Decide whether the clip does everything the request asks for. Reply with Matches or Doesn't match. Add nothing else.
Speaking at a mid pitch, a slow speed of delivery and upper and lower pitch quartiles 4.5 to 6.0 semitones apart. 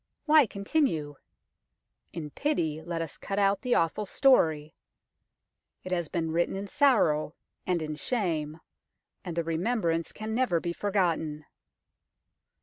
Matches